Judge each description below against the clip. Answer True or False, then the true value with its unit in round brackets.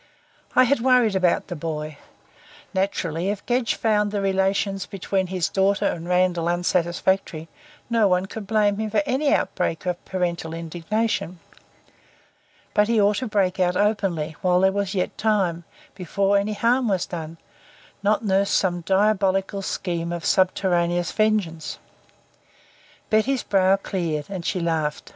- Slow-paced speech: False (145 wpm)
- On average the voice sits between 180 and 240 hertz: True (190 Hz)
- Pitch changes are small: False (3.1 semitones)